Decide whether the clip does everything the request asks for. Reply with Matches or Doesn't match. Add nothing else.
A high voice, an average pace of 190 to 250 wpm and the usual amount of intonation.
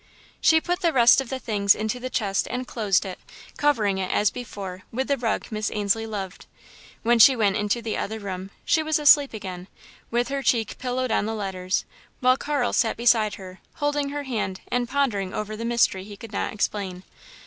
Matches